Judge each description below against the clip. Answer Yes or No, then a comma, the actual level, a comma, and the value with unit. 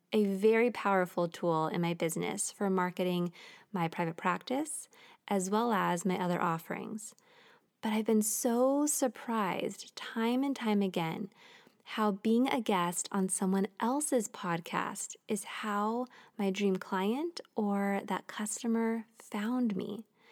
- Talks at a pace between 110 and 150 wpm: Yes, slow, 135 wpm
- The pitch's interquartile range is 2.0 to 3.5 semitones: No, average, 3.9 semitones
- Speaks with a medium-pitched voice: No, high, 210 Hz